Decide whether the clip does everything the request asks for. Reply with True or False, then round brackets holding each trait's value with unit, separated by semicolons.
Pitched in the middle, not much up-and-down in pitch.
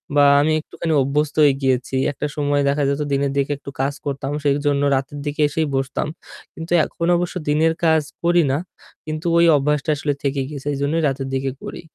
True (145 Hz; 1.9 semitones)